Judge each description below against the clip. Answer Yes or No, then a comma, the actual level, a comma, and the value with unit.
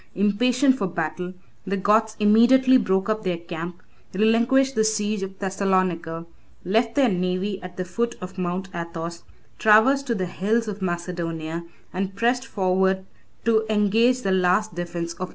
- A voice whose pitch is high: Yes, high, 195 Hz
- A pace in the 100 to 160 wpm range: Yes, average, 150 wpm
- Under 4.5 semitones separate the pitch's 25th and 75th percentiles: Yes, average, 3.5 semitones